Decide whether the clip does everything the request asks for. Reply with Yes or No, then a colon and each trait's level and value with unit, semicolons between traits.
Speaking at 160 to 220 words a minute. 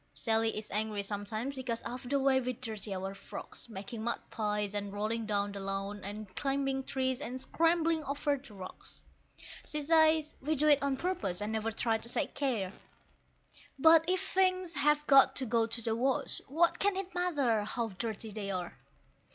Yes: average, 185 wpm